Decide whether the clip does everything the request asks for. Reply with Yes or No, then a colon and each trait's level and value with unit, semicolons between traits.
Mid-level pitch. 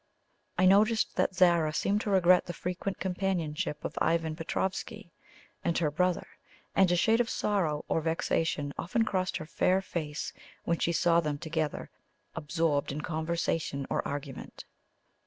Yes: medium, 170 Hz